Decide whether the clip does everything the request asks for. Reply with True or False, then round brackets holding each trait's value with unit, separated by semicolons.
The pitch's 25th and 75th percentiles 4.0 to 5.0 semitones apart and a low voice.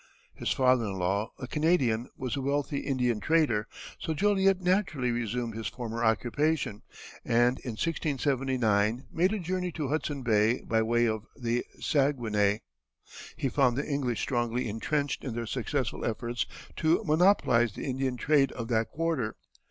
True (4.4 semitones; 125 Hz)